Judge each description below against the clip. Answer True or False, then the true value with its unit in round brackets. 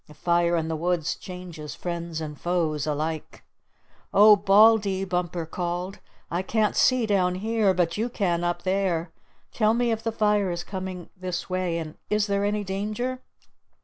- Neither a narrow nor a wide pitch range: True (3.4 semitones)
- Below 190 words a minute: True (165 wpm)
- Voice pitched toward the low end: False (185 Hz)